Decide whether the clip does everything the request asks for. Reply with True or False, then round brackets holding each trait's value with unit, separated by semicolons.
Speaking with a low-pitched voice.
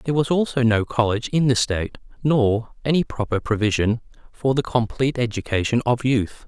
True (120 Hz)